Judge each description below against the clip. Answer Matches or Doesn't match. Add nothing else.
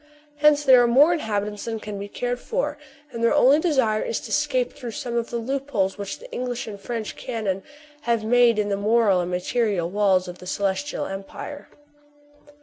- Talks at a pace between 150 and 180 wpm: Doesn't match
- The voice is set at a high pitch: Matches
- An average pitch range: Matches